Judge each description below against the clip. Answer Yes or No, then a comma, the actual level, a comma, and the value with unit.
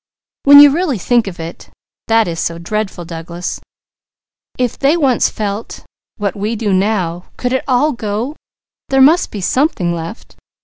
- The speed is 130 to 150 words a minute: No, average, 160 wpm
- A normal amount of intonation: No, wide, 6.7 semitones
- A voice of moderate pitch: No, high, 215 Hz